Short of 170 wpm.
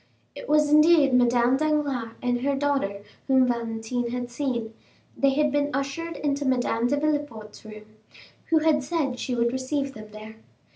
Yes: average, 160 wpm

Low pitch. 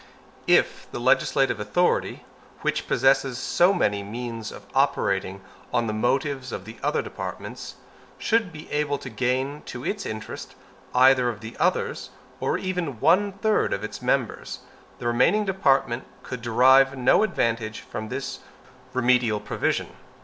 Yes: low, 130 Hz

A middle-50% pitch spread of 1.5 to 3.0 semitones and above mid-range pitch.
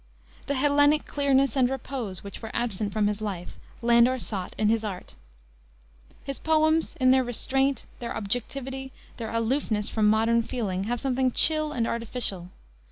No: average, 3.8 semitones; high, 240 Hz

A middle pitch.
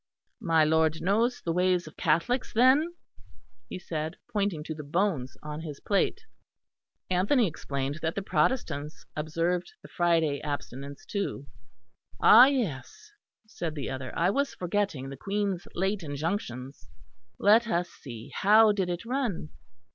Yes: medium, 175 Hz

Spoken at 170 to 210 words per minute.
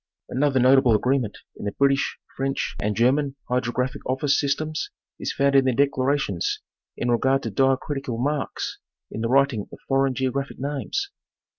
No: average, 150 wpm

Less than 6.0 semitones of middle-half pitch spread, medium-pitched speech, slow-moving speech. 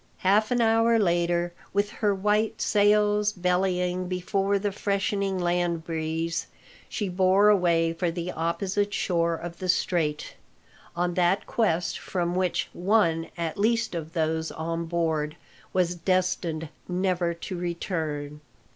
Yes: average, 2.9 semitones; medium, 180 Hz; slow, 130 wpm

